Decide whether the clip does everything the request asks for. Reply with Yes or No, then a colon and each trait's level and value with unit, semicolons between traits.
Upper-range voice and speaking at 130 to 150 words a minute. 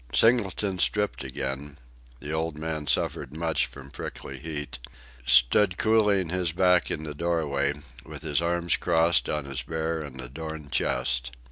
No: very low, 80 Hz; average, 145 wpm